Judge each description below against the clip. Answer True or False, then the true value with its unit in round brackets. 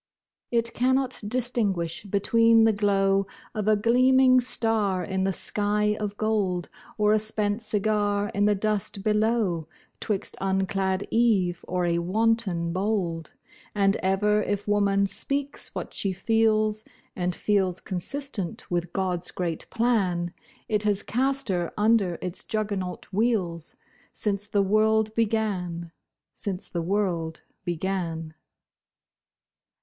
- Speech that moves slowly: True (120 wpm)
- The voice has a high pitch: True (205 Hz)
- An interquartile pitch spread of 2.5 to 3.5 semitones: True (3.0 semitones)